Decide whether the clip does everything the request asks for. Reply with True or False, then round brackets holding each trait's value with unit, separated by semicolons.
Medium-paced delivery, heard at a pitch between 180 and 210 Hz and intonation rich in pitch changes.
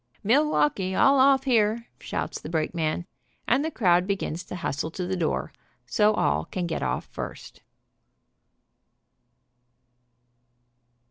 False (120 wpm; 190 Hz; 5.9 semitones)